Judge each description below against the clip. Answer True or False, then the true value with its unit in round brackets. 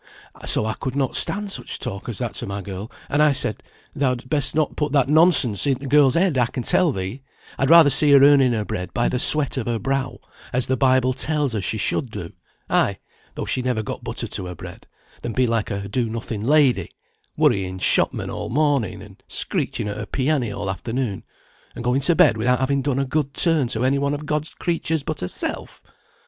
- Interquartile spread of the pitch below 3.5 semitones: False (4.3 semitones)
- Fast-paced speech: True (215 wpm)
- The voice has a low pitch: True (130 Hz)